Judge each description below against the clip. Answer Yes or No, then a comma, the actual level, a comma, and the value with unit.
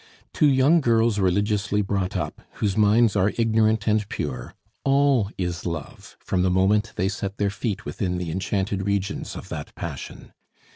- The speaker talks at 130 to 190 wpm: Yes, average, 160 wpm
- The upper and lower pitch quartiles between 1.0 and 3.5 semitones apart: Yes, average, 2.8 semitones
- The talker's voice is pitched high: No, low, 100 Hz